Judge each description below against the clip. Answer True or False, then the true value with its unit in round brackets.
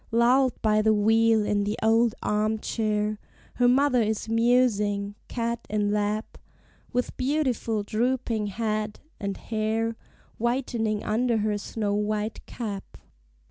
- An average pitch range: False (2.0 semitones)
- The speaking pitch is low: False (220 Hz)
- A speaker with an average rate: False (125 wpm)